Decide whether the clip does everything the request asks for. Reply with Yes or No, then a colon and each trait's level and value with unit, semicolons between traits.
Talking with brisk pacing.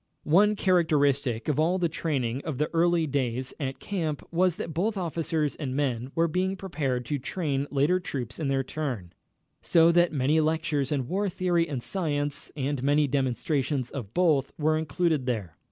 No: average, 170 wpm